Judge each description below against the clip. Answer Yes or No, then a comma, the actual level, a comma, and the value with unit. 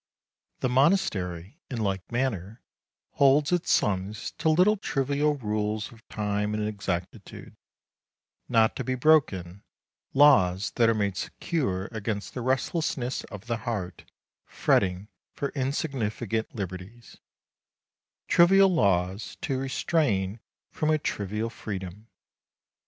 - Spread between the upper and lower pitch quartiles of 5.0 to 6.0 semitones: Yes, wide, 5.6 semitones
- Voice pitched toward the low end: Yes, low, 110 Hz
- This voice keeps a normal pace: No, slow, 115 wpm